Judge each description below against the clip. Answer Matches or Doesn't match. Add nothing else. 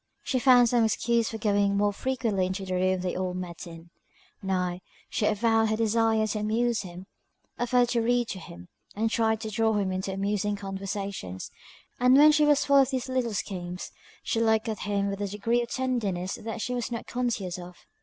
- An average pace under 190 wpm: Doesn't match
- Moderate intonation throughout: Matches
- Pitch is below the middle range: Doesn't match